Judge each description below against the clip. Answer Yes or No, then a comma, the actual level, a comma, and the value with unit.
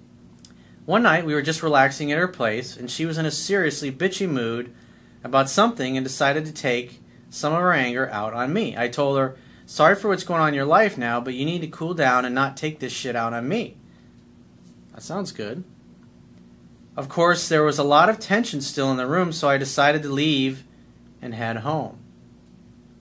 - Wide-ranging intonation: No, average, 4.9 semitones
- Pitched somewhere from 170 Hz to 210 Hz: No, low, 135 Hz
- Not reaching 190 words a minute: No, fast, 205 wpm